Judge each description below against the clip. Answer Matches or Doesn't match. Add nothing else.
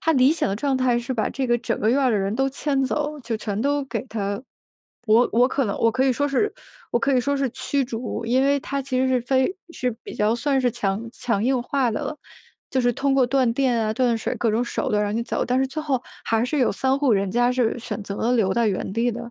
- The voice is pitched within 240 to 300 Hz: Matches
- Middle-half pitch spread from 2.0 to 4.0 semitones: Matches